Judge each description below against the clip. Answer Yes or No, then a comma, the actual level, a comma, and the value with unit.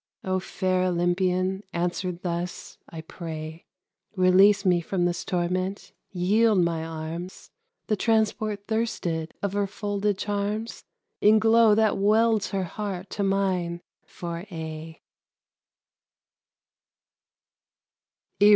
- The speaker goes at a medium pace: No, slow, 105 wpm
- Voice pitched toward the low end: No, medium, 185 Hz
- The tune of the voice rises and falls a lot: No, average, 3.0 semitones